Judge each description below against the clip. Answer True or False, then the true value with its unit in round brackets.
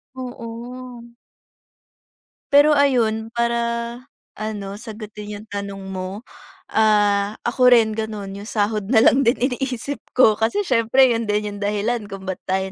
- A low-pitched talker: False (220 Hz)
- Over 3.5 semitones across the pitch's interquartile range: False (3.0 semitones)